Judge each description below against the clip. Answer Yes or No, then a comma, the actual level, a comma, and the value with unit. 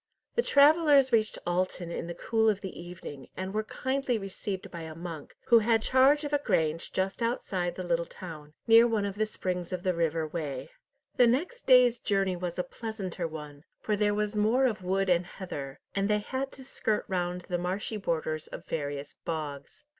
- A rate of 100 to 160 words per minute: No, average, 195 wpm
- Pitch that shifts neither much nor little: Yes, average, 5.0 semitones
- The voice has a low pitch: No, high, 190 Hz